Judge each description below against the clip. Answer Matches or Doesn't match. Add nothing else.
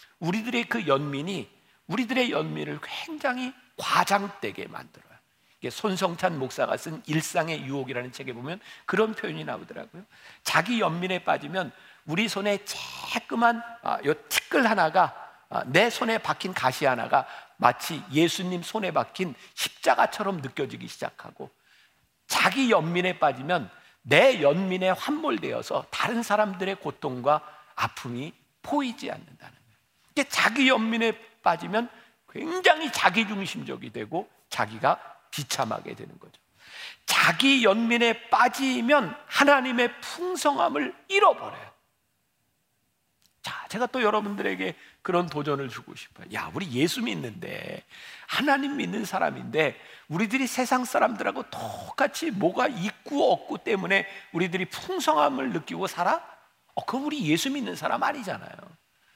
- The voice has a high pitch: Matches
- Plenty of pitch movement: Matches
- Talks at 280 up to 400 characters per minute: Matches